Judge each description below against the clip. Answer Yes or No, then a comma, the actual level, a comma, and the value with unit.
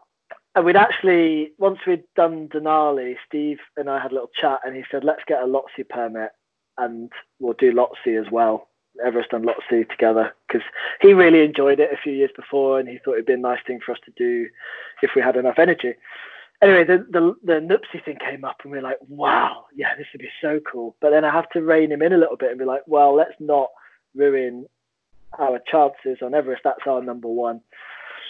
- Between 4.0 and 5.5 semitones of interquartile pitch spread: Yes, average, 4.9 semitones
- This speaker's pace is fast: Yes, fast, 220 wpm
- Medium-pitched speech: Yes, medium, 145 Hz